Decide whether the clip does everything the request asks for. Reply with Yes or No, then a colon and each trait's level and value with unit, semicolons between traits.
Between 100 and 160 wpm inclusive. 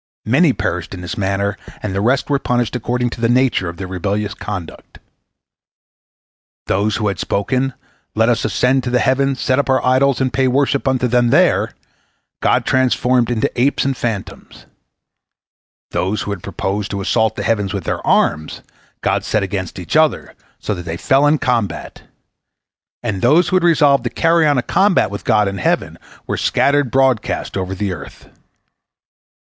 No: average, 175 wpm